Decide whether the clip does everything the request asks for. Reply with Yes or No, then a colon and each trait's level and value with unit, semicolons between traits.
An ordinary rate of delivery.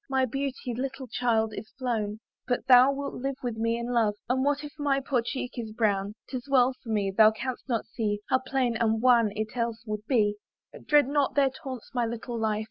No: fast, 215 wpm